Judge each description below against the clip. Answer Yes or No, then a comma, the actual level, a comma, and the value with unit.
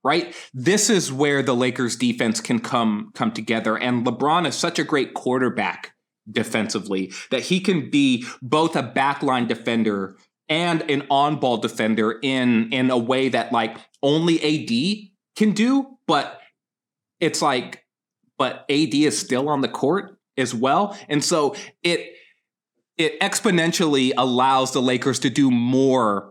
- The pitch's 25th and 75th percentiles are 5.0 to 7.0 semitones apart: Yes, average, 5.3 semitones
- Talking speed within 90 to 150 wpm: Yes, average, 145 wpm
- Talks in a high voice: No, low, 135 Hz